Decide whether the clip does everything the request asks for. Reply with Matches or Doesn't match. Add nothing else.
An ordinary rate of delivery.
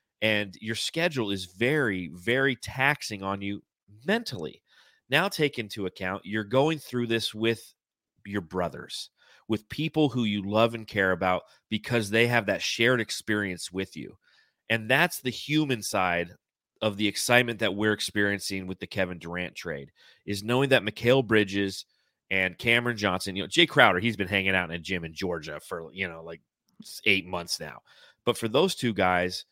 Matches